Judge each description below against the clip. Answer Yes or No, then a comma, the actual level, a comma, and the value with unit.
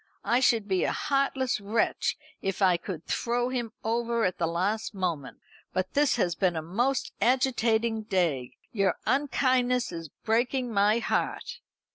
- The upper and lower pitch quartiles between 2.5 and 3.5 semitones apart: No, average, 4.9 semitones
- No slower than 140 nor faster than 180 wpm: Yes, average, 150 wpm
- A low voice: No, high, 220 Hz